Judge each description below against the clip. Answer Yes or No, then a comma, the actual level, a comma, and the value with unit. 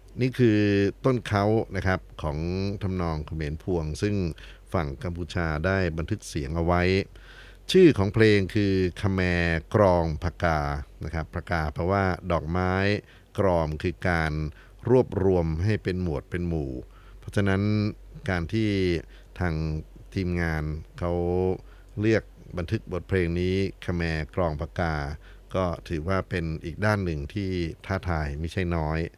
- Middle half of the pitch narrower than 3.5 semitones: Yes, average, 3.0 semitones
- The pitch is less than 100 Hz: Yes, very low, 90 Hz